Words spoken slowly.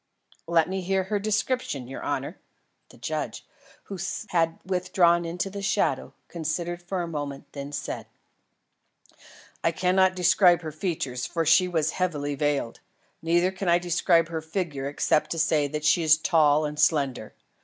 No: average, 155 wpm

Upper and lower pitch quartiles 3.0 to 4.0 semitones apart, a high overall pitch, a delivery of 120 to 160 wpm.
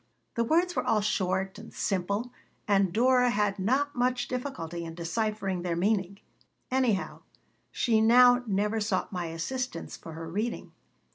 No: average, 4.9 semitones; high, 210 Hz; average, 145 wpm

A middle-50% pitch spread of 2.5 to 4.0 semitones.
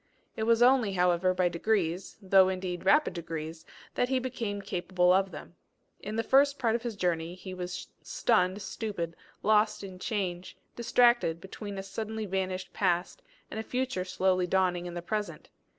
Yes: average, 3.6 semitones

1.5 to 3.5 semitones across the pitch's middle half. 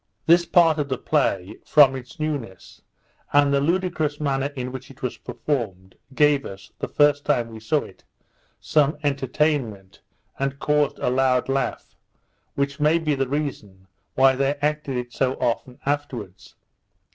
Yes: average, 2.9 semitones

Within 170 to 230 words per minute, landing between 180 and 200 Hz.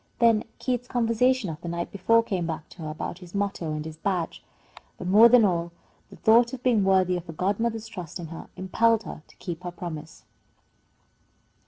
Yes: average, 195 wpm; high, 190 Hz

